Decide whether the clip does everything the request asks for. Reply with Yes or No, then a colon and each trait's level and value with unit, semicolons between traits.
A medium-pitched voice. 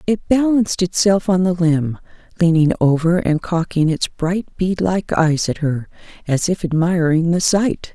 Yes: medium, 175 Hz